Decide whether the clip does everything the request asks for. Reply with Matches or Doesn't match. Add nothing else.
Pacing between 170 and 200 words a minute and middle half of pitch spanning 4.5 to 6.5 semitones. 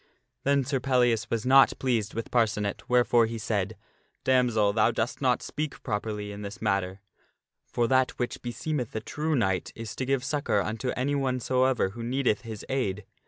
Doesn't match